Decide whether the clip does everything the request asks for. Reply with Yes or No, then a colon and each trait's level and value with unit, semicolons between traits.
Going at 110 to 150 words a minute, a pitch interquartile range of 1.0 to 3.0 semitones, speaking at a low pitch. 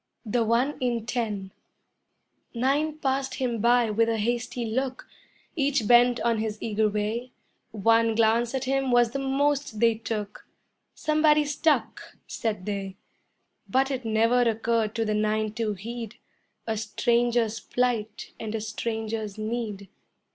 No: average, 140 wpm; narrow, 2.4 semitones; high, 230 Hz